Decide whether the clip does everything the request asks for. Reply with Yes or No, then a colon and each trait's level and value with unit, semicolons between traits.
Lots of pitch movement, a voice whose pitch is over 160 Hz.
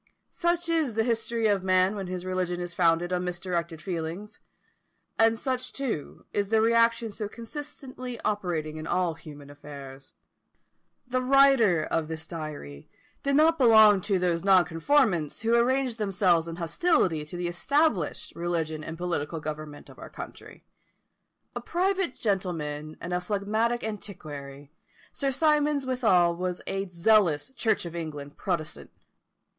Yes: wide, 6.1 semitones; medium, 185 Hz